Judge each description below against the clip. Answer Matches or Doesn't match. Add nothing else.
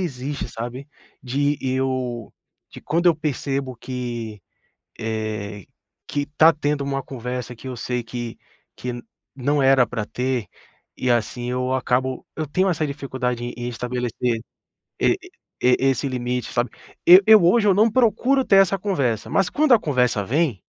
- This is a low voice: Matches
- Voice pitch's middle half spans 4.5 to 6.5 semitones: Doesn't match